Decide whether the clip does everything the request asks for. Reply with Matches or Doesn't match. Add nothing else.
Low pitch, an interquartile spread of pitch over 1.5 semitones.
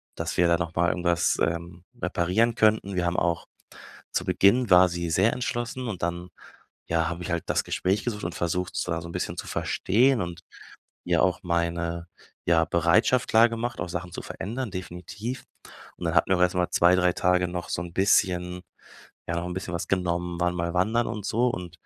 Matches